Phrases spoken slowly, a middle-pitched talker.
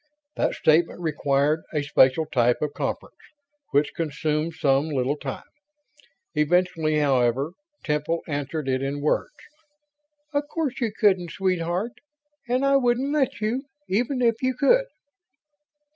Yes: slow, 130 wpm; medium, 160 Hz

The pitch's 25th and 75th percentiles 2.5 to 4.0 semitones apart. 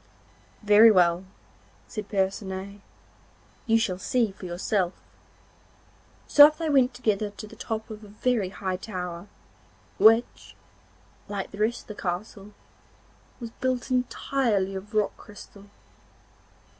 Yes: average, 3.0 semitones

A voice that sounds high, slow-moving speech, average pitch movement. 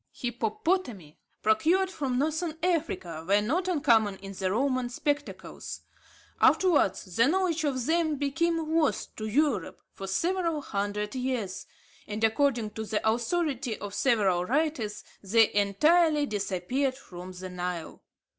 No: high, 245 Hz; slow, 125 wpm; wide, 7.2 semitones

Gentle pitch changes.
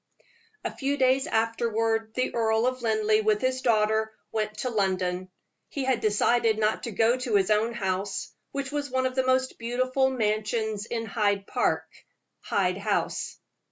No: average, 3.2 semitones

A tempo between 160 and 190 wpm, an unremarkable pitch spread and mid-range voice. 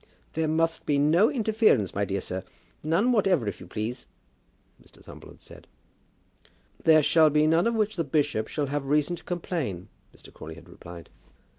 No: average, 175 wpm; wide, 7.9 semitones; medium, 150 Hz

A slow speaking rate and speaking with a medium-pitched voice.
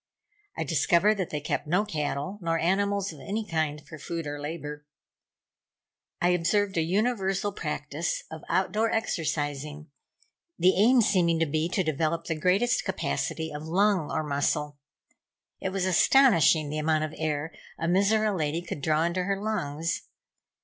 No: average, 155 wpm; medium, 165 Hz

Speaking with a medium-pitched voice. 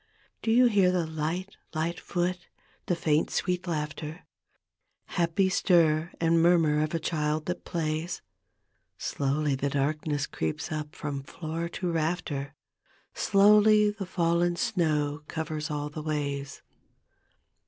Yes: medium, 160 Hz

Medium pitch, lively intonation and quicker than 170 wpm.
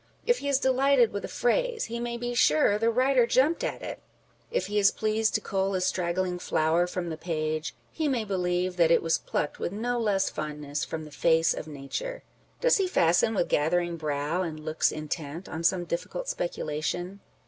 Yes: medium, 180 Hz; wide, 6.6 semitones; average, 195 wpm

